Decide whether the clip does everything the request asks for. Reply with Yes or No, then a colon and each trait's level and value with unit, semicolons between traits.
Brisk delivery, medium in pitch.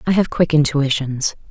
No: average, 160 wpm; medium, 150 Hz